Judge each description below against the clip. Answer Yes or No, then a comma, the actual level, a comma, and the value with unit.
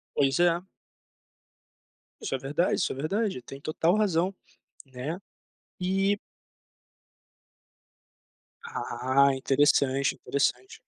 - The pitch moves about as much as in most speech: No, wide, 5.8 semitones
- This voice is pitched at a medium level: Yes, medium, 155 Hz